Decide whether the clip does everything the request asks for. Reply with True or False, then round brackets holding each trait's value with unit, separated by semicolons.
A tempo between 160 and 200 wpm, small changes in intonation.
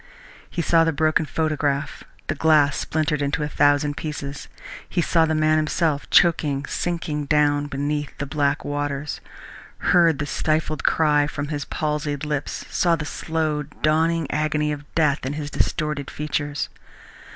False (150 wpm; 1.4 semitones)